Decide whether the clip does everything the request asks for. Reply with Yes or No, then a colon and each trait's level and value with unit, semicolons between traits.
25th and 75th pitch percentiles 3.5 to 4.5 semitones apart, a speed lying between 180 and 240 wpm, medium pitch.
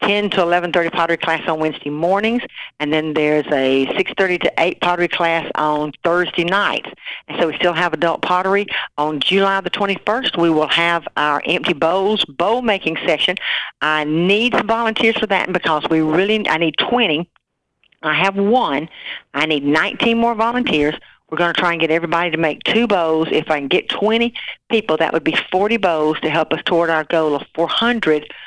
Yes: average, 4.1 semitones; average, 190 wpm; medium, 170 Hz